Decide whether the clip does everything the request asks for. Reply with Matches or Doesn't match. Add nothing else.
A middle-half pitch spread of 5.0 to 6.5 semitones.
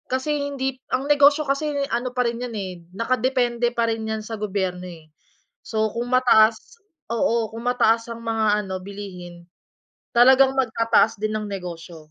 Doesn't match